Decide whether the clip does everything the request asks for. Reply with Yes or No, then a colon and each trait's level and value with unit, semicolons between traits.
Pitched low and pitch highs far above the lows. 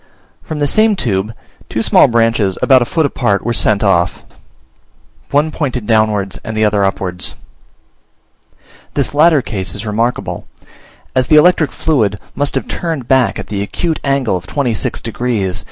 Yes: low, 115 Hz; wide, 5.8 semitones